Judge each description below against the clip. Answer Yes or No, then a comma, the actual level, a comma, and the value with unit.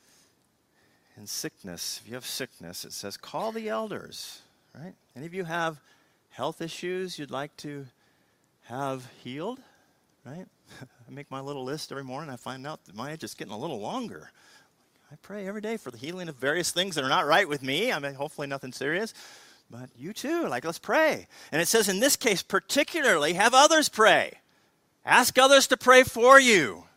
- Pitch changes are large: Yes, wide, 8.5 semitones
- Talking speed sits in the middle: Yes, average, 190 wpm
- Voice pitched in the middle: Yes, medium, 165 Hz